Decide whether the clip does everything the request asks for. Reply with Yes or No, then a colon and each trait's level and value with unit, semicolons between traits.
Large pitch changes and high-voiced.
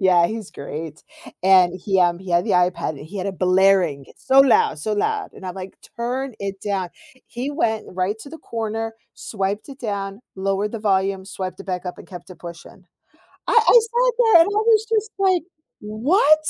Yes: wide, 6.0 semitones; high, 200 Hz